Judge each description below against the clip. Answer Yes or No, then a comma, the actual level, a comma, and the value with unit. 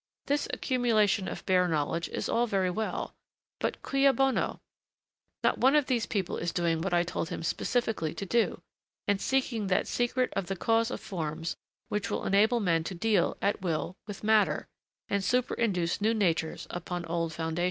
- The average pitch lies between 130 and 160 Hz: No, high, 195 Hz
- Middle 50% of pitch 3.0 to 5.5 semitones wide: Yes, average, 5.0 semitones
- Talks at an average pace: Yes, average, 180 wpm